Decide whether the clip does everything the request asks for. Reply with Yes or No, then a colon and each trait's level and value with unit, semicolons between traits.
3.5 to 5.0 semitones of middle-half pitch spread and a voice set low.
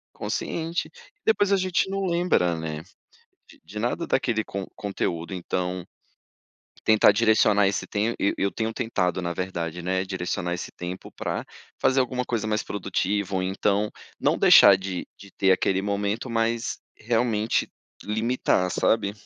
Yes: average, 3.8 semitones; low, 100 Hz